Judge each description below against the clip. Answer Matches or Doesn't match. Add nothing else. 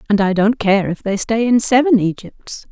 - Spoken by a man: Doesn't match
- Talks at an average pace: Doesn't match